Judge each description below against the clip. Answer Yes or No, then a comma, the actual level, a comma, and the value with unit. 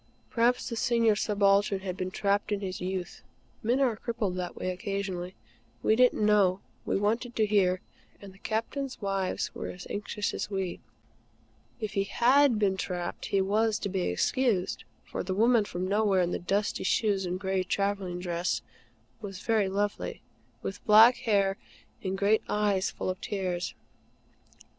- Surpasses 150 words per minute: Yes, average, 160 wpm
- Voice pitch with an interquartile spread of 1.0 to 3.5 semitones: Yes, narrow, 2.5 semitones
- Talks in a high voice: Yes, high, 200 Hz